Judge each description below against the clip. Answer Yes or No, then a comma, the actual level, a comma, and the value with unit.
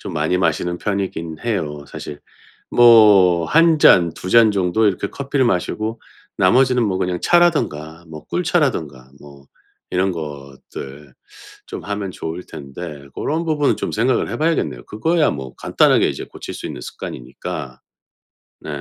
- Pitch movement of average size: No, wide, 7.5 semitones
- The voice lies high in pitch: No, very low, 95 Hz